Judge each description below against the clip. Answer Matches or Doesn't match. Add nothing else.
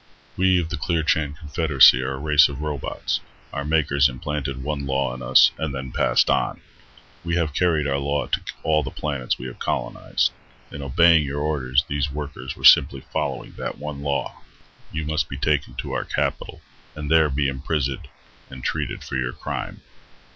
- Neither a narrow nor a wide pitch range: Doesn't match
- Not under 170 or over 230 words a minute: Matches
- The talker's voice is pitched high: Doesn't match